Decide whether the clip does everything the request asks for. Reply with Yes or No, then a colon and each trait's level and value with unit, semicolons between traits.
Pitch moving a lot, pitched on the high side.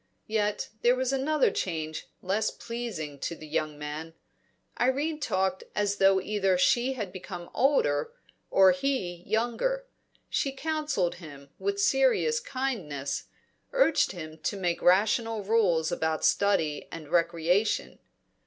Yes: wide, 7.7 semitones; high, 195 Hz